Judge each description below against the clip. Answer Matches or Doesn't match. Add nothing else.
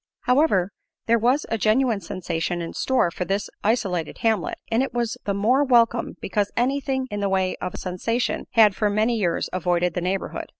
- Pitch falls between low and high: Doesn't match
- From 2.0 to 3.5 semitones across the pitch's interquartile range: Doesn't match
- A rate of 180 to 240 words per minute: Matches